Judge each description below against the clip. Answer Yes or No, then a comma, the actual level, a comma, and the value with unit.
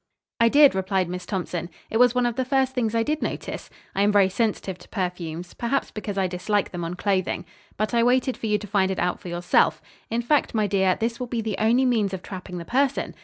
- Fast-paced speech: Yes, fast, 240 wpm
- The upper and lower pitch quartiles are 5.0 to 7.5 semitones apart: No, average, 4.3 semitones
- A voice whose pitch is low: No, high, 210 Hz